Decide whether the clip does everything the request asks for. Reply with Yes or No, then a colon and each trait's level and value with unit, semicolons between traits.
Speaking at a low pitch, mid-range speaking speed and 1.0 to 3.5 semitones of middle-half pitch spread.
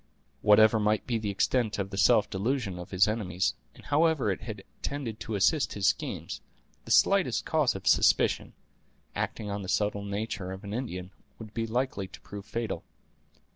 Yes: low, 105 Hz; average, 175 wpm; narrow, 2.6 semitones